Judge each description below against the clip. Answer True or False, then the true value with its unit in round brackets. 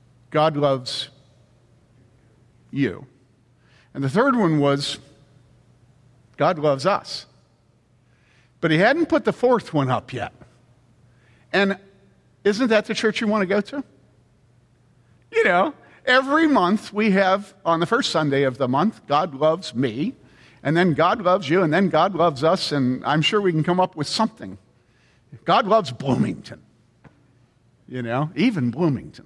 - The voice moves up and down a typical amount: False (7.8 semitones)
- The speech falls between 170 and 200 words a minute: False (150 wpm)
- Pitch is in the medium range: True (145 Hz)